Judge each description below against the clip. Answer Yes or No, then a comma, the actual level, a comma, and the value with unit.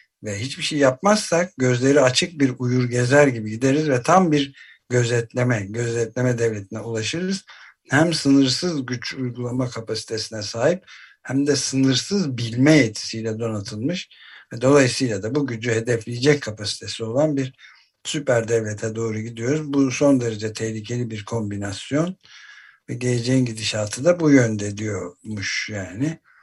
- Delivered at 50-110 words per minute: No, average, 125 wpm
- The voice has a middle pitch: No, low, 125 Hz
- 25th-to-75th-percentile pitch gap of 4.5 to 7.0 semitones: No, average, 4.1 semitones